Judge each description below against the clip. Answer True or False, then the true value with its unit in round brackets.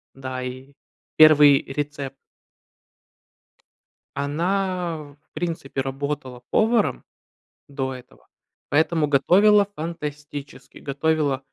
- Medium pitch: True (145 Hz)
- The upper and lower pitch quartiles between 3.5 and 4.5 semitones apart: False (3.0 semitones)